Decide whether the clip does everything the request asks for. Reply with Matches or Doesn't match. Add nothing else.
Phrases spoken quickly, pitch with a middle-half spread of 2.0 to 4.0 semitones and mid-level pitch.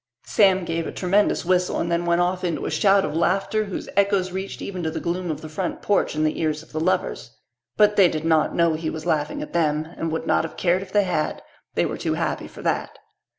Matches